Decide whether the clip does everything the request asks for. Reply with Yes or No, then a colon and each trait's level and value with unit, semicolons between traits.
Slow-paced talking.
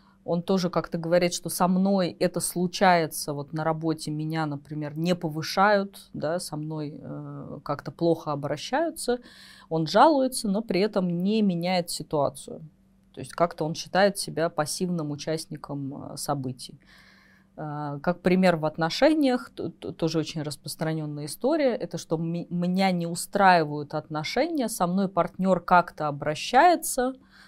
No: average, 125 wpm